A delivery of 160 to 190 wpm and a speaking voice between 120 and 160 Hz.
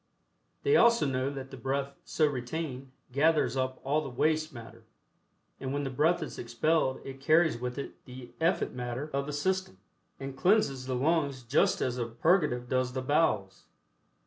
Yes: average, 170 wpm; low, 135 Hz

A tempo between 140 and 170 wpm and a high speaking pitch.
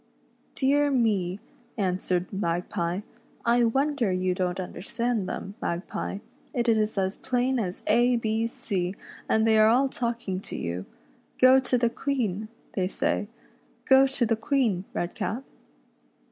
Yes: average, 150 wpm; high, 220 Hz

